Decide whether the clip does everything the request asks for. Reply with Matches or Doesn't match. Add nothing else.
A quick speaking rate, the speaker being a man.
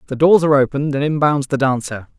Matches